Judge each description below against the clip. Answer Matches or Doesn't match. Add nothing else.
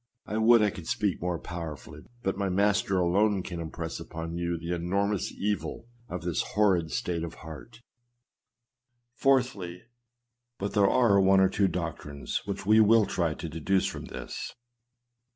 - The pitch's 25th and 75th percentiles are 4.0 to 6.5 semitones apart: Doesn't match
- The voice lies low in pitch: Matches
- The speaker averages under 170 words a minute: Matches